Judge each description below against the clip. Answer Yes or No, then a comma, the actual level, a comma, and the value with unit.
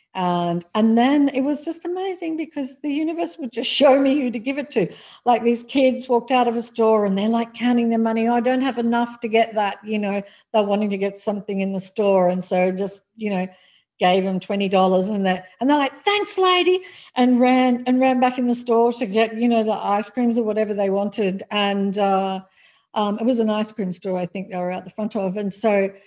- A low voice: No, high, 225 Hz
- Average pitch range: Yes, average, 4.2 semitones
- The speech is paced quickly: Yes, fast, 240 wpm